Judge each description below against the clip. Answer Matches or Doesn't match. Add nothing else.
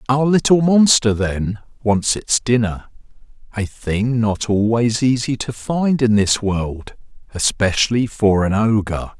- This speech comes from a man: Matches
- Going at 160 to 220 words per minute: Doesn't match